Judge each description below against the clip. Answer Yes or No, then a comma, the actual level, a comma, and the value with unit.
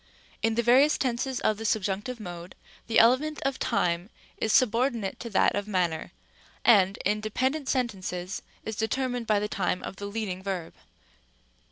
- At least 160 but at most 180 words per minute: Yes, average, 165 wpm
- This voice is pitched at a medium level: No, high, 215 Hz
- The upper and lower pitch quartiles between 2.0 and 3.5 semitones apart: No, average, 4.2 semitones